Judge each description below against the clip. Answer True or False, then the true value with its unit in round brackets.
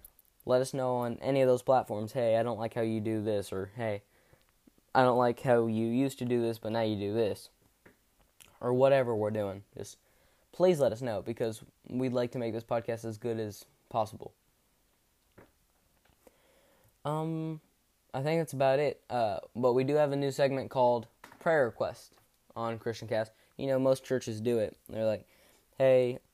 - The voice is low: True (120 Hz)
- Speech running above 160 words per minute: True (185 wpm)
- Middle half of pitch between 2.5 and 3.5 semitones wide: True (2.9 semitones)